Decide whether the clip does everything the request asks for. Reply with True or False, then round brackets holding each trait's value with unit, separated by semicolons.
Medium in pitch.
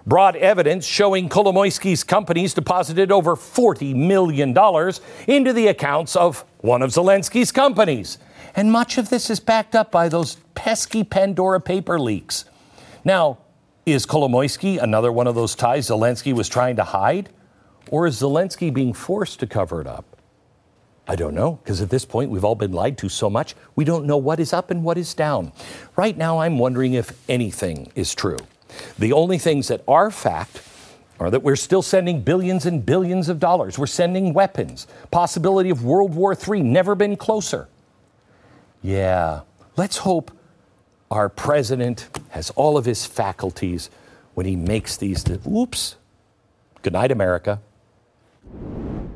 True (160 Hz)